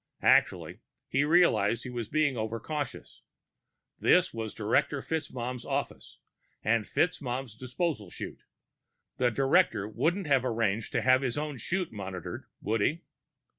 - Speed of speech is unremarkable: No, slow, 130 wpm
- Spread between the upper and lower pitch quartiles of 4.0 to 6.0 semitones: Yes, average, 5.0 semitones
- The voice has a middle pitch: No, low, 125 Hz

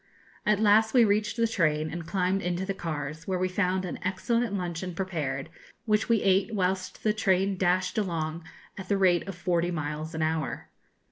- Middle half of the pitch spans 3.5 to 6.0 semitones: No, average, 3.1 semitones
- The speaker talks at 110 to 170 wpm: No, average, 185 wpm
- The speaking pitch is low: No, medium, 185 Hz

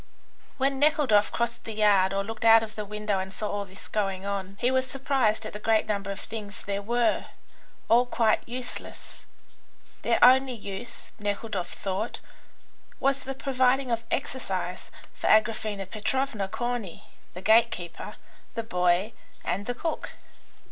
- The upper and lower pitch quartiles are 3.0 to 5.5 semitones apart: Yes, average, 3.5 semitones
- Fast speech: No, average, 155 wpm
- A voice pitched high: Yes, high, 220 Hz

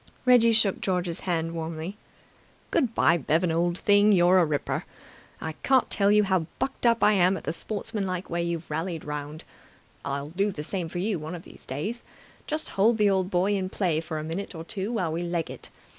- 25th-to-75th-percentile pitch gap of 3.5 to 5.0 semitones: Yes, average, 3.9 semitones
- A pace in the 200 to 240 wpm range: Yes, fast, 205 wpm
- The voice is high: No, medium, 180 Hz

